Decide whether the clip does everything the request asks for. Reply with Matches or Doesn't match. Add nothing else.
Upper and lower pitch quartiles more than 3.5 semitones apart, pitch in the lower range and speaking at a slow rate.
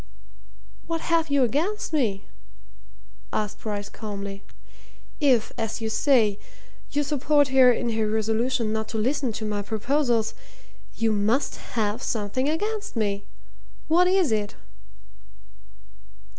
Doesn't match